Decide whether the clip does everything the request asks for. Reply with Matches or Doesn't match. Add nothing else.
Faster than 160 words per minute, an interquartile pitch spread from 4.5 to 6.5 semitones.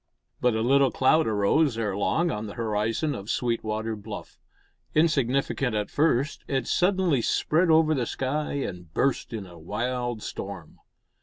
Doesn't match